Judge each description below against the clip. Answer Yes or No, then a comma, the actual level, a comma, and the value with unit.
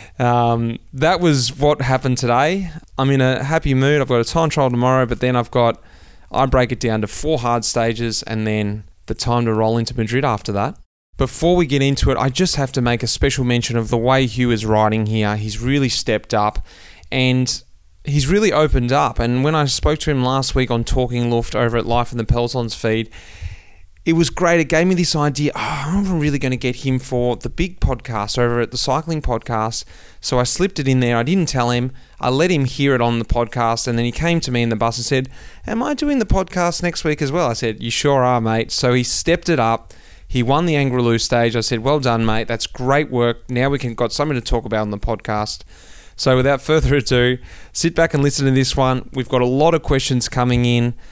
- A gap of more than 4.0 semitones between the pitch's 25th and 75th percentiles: No, average, 3.5 semitones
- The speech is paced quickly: Yes, fast, 240 wpm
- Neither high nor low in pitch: No, low, 125 Hz